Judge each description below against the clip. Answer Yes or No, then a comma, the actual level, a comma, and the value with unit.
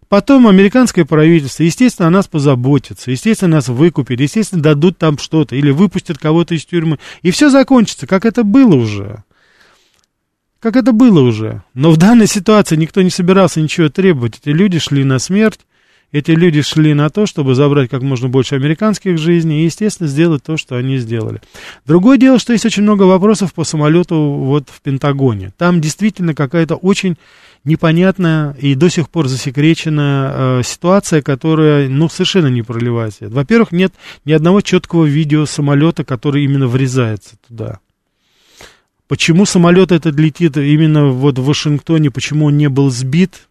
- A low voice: No, medium, 155 Hz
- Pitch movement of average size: Yes, average, 4.7 semitones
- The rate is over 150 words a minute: Yes, fast, 160 wpm